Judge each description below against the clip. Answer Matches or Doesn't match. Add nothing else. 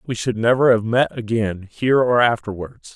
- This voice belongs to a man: Matches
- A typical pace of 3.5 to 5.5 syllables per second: Matches